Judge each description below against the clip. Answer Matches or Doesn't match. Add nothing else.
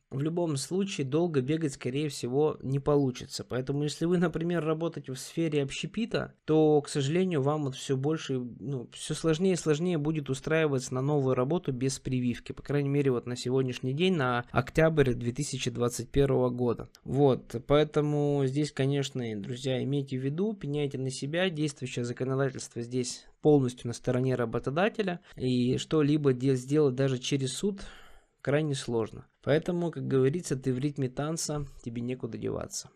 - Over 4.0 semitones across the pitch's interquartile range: Doesn't match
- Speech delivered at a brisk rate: Doesn't match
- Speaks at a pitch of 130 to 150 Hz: Matches